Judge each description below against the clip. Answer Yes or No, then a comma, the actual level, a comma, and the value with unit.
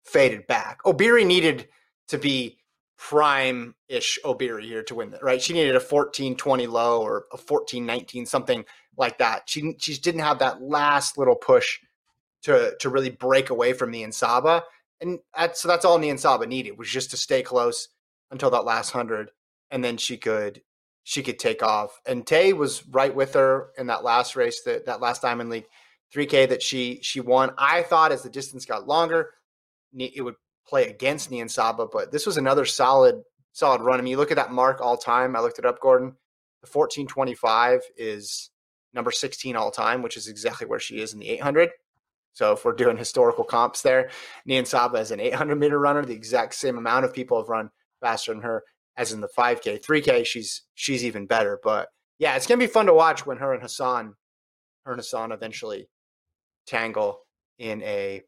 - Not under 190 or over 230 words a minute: Yes, average, 200 wpm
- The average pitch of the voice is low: No, medium, 145 Hz